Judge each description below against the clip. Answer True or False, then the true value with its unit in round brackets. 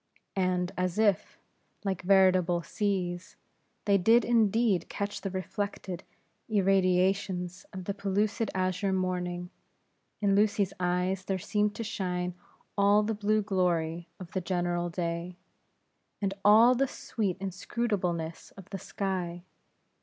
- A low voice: False (190 Hz)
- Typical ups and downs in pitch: False (2.3 semitones)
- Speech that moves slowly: True (125 wpm)